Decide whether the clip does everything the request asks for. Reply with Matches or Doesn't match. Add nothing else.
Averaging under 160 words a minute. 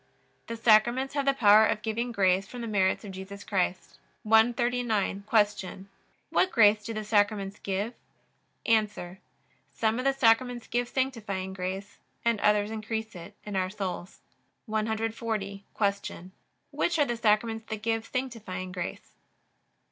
Matches